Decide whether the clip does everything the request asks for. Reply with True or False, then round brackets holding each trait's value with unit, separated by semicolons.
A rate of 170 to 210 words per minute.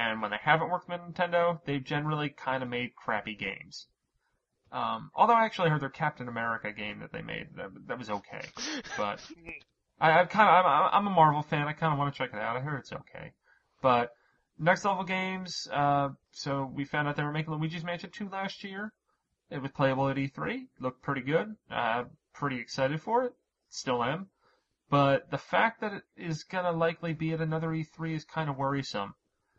True (200 wpm)